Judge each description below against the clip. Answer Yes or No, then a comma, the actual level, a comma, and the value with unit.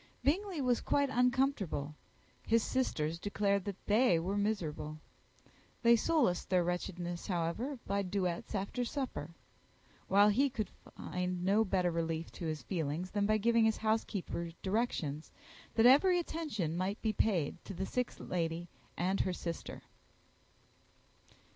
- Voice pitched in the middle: No, high, 195 Hz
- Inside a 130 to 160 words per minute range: Yes, average, 140 wpm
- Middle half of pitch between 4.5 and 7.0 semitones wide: Yes, average, 5.2 semitones